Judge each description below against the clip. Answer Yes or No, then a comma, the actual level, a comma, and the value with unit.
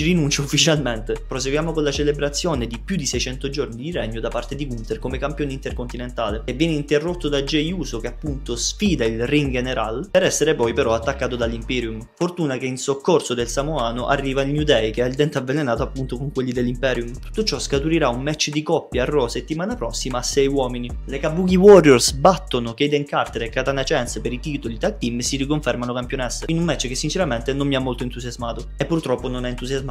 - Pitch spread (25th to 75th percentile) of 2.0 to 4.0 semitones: Yes, average, 3.4 semitones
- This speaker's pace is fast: Yes, fast, 210 wpm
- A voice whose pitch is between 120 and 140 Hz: Yes, low, 135 Hz